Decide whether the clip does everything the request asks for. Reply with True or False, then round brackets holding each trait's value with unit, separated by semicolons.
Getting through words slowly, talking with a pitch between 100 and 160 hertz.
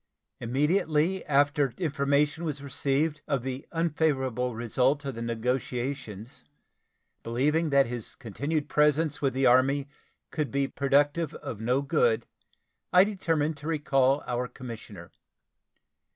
True (120 wpm; 140 Hz)